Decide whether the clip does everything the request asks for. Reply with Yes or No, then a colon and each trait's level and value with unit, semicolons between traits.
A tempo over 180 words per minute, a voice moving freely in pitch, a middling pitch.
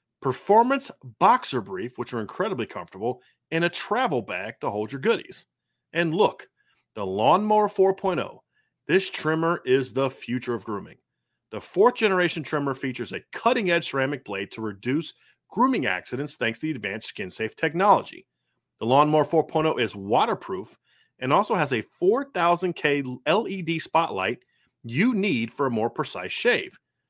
No: average, 150 wpm; wide, 6.3 semitones; medium, 155 Hz